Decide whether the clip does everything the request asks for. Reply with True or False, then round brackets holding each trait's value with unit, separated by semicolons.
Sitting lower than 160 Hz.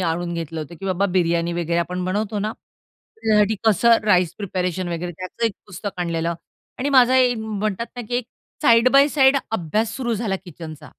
False (195 Hz)